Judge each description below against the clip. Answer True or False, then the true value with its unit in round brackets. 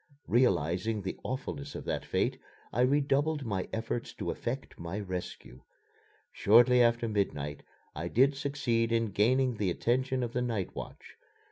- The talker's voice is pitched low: True (115 Hz)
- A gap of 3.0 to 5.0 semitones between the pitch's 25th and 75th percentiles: True (4.5 semitones)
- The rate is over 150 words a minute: False (145 wpm)